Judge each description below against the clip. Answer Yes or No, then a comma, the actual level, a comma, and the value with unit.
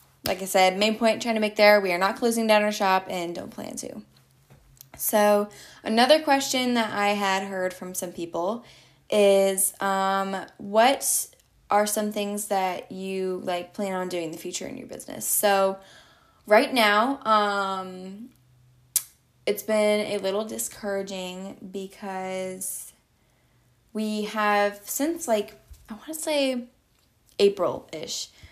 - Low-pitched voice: No, high, 200 Hz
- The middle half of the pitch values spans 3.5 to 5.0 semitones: No, narrow, 2.5 semitones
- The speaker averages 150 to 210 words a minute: No, average, 140 wpm